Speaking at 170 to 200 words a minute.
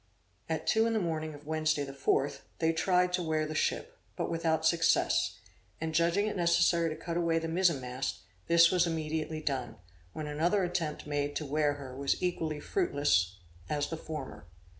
Yes: average, 185 wpm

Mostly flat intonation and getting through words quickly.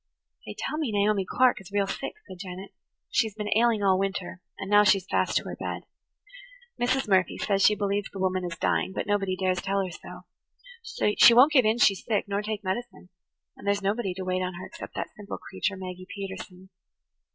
Yes: narrow, 2.2 semitones; fast, 210 wpm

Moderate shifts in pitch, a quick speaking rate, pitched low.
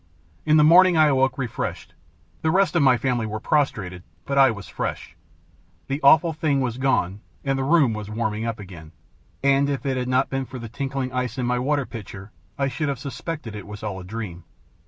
Yes: average, 4.3 semitones; fast, 210 wpm; low, 130 Hz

